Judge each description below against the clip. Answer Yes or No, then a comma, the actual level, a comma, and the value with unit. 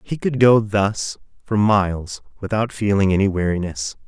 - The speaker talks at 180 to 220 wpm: No, average, 145 wpm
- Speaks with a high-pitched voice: No, low, 100 Hz